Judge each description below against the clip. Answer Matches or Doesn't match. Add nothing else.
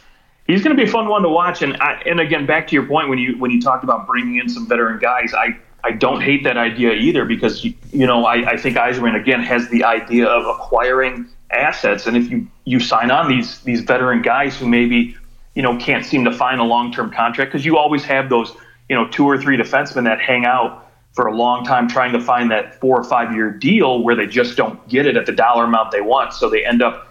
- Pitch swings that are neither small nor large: Matches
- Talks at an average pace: Doesn't match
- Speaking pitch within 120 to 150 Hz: Matches